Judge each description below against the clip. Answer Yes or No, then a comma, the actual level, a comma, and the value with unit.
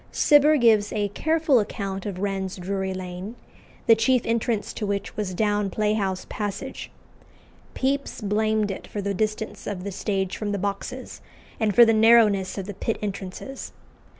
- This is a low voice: No, high, 205 Hz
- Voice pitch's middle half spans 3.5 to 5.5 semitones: No, narrow, 2.4 semitones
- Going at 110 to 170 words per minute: Yes, average, 160 wpm